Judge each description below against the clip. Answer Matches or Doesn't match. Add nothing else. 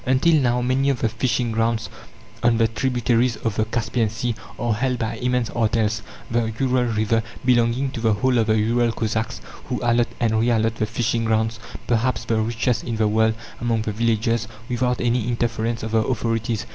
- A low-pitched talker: Matches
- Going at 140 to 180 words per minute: Doesn't match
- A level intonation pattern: Matches